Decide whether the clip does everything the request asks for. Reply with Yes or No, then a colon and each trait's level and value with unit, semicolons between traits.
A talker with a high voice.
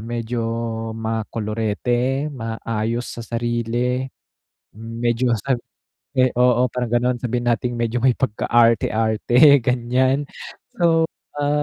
No: low, 120 Hz